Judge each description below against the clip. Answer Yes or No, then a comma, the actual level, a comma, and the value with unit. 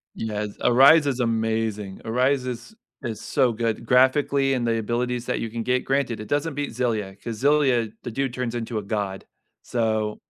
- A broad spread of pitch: No, average, 2.9 semitones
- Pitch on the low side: Yes, low, 120 Hz